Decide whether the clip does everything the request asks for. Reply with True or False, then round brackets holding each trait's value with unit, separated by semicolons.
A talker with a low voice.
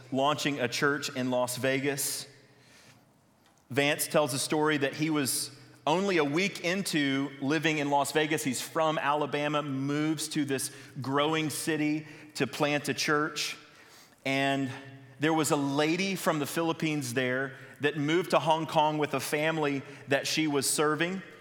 False (145 Hz)